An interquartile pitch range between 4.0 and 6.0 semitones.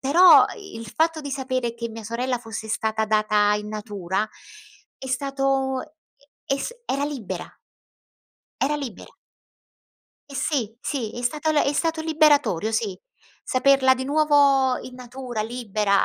Yes: average, 4.3 semitones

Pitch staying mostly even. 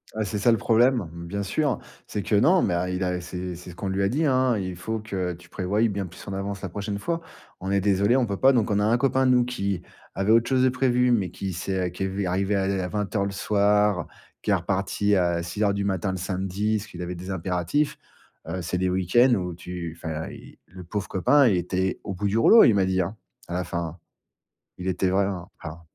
No: average, 3.1 semitones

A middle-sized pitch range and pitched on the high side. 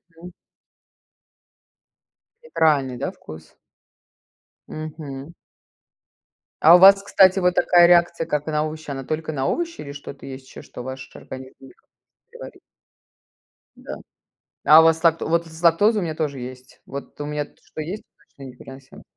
No: average, 4.0 semitones; medium, 155 Hz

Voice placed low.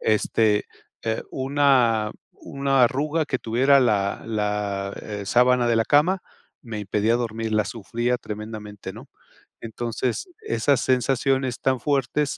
Yes: low, 120 Hz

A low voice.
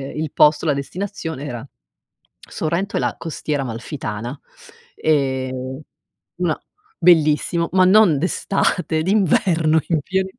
No: medium, 155 Hz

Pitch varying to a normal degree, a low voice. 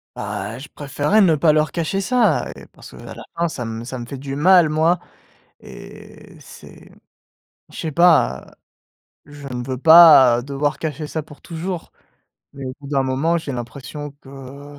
No: average, 3.5 semitones; medium, 145 Hz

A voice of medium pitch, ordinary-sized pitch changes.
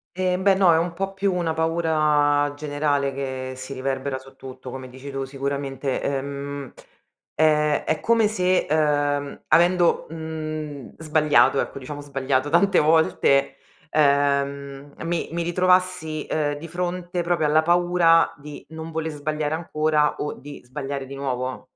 Yes: medium, 150 Hz; average, 3.0 semitones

